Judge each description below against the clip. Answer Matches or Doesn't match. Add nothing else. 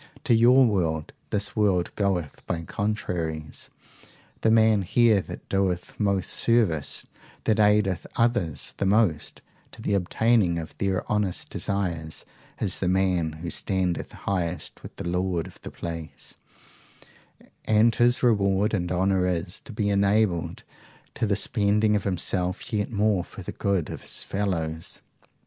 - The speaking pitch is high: Doesn't match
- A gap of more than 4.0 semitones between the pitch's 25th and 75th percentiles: Doesn't match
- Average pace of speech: Matches